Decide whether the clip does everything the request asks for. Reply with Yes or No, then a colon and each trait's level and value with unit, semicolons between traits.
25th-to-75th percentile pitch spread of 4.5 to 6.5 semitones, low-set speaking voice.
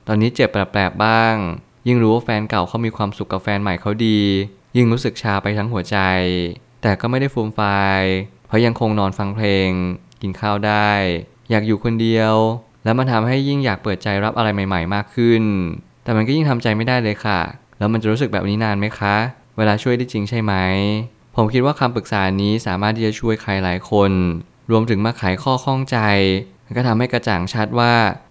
No: average, 2.8 semitones; low, 110 Hz